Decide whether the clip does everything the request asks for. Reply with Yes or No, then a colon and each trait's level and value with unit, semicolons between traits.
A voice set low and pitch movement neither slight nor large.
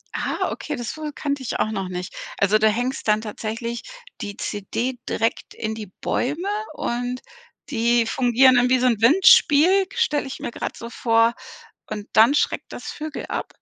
No: high, 240 Hz; average, 4.3 semitones